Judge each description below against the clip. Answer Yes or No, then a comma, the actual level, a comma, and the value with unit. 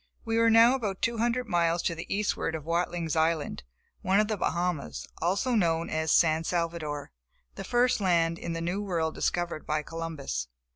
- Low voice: No, medium, 170 Hz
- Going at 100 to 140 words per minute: No, average, 180 wpm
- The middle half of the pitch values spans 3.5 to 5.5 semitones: Yes, average, 4.1 semitones